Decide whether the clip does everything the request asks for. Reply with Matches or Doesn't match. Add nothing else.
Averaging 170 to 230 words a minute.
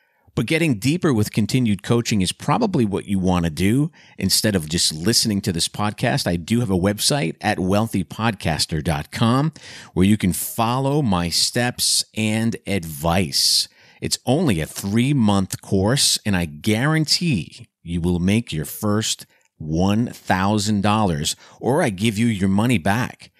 Doesn't match